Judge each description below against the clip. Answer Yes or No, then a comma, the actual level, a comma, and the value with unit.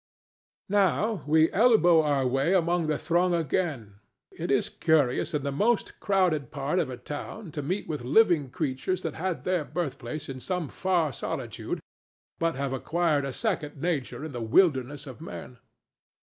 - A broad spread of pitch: No, average, 4.5 semitones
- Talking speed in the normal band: Yes, average, 160 wpm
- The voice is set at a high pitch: No, medium, 155 Hz